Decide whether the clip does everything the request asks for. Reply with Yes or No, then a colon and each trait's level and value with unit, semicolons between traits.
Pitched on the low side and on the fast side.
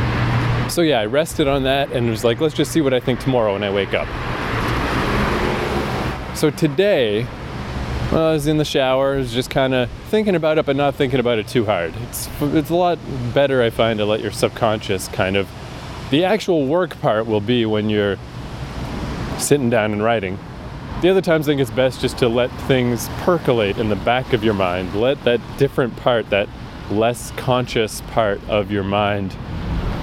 No: low, 120 Hz; average, 195 wpm